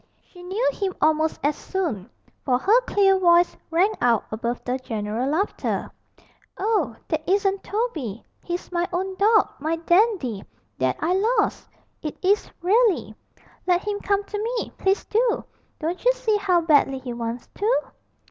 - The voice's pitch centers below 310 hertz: No, very high, 360 Hz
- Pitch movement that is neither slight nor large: No, wide, 6.6 semitones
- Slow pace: No, average, 155 wpm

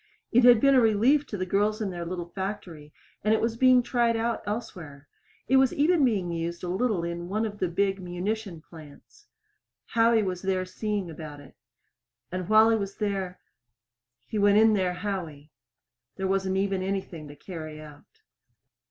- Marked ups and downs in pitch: No, average, 4.2 semitones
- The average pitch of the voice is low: No, high, 195 Hz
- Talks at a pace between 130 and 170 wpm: No, average, 180 wpm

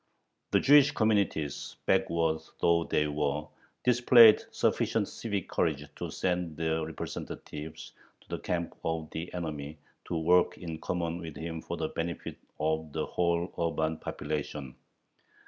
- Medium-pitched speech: No, very low, 80 Hz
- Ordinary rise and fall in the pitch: No, narrow, 2.0 semitones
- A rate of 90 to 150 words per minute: Yes, slow, 135 wpm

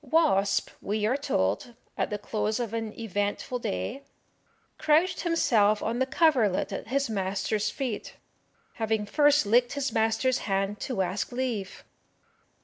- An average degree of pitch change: Yes, average, 4.2 semitones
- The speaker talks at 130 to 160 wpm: Yes, average, 140 wpm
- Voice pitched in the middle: No, high, 225 Hz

